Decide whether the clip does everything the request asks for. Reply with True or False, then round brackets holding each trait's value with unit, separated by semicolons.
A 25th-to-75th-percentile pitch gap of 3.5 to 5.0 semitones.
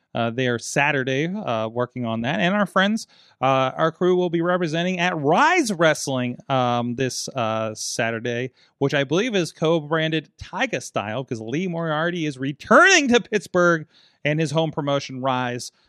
False (5.6 semitones)